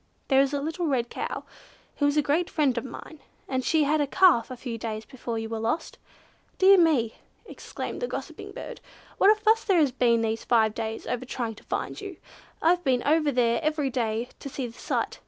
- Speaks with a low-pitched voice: No, very high, 265 Hz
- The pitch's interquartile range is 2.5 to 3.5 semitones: No, average, 5.2 semitones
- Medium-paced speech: No, fast, 215 wpm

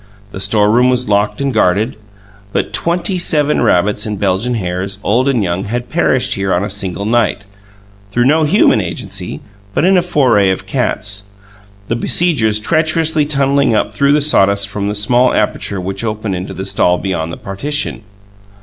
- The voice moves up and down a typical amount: No, wide, 5.9 semitones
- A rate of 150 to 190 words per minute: Yes, average, 170 wpm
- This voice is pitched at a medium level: No, low, 110 Hz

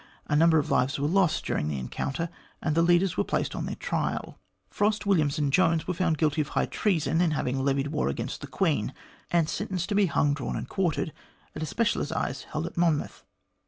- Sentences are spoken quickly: Yes, fast, 215 wpm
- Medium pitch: Yes, medium, 160 Hz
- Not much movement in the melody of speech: No, average, 3.6 semitones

